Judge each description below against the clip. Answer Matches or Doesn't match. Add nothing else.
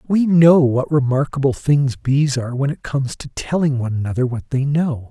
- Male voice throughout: Matches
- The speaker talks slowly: Doesn't match